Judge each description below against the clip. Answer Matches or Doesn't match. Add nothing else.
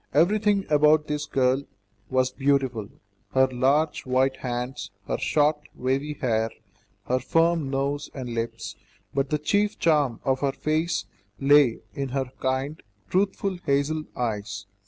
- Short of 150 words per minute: Matches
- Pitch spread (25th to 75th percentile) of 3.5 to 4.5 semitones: Doesn't match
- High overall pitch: Doesn't match